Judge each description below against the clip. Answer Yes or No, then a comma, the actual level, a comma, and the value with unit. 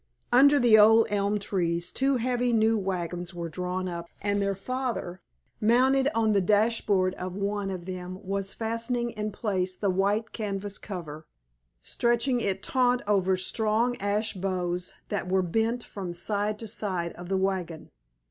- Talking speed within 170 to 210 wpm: No, average, 160 wpm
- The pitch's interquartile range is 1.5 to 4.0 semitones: Yes, average, 3.5 semitones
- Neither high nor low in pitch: No, high, 200 Hz